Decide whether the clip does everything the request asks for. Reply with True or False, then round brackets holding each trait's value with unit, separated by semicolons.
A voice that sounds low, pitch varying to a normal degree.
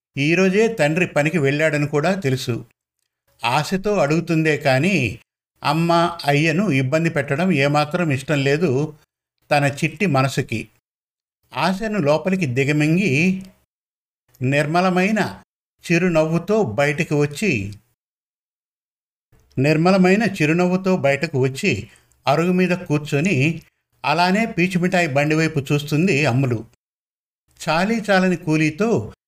False (155 Hz; 4.2 semitones)